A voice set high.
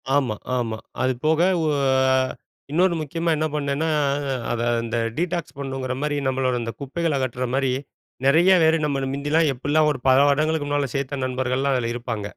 No: medium, 140 Hz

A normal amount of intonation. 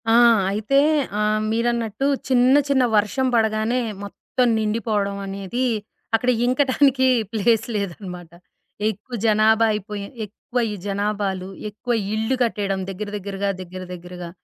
Yes: average, 3.2 semitones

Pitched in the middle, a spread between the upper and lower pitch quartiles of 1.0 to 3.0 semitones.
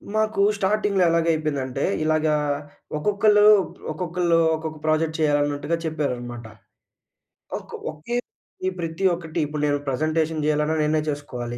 Yes: medium, 155 Hz; narrow, 2.5 semitones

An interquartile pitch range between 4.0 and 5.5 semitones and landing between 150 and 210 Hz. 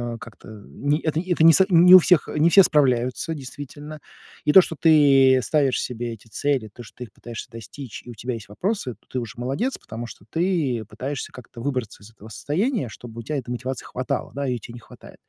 No: average, 4.6 semitones; low, 130 Hz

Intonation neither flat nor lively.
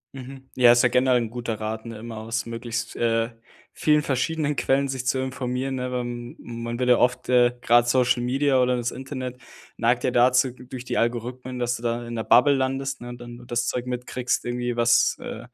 No: narrow, 1.4 semitones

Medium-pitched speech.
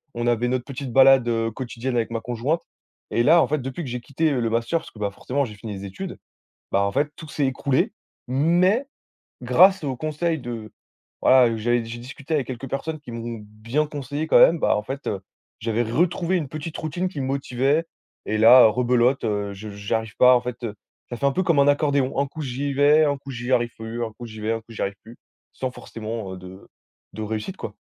No: low, 125 Hz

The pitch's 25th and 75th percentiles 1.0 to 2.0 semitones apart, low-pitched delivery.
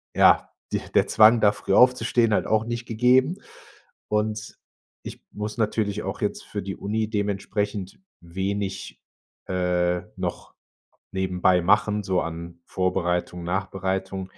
No: average, 2.7 semitones; low, 100 Hz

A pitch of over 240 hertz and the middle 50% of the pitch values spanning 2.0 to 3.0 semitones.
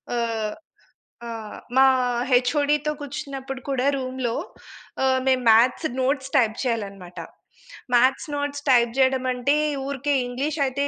Yes: very high, 260 Hz; average, 2.7 semitones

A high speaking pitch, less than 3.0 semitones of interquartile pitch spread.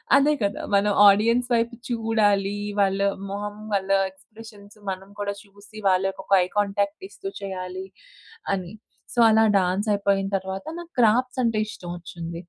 Yes: high, 200 Hz; narrow, 2.4 semitones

